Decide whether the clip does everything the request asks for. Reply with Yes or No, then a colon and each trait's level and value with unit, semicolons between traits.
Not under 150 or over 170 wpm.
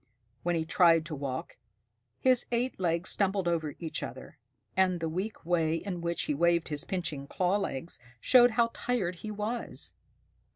Yes: average, 165 wpm